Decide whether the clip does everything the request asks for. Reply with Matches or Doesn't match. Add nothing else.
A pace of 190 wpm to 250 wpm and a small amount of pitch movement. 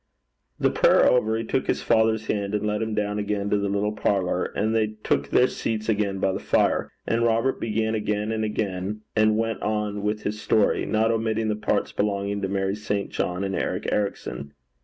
Matches